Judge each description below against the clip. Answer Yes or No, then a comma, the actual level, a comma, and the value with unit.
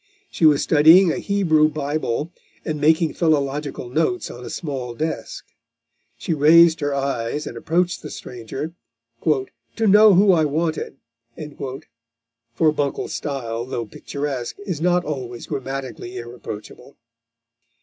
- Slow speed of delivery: Yes, slow, 125 wpm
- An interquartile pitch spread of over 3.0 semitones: Yes, average, 3.8 semitones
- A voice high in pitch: No, medium, 150 Hz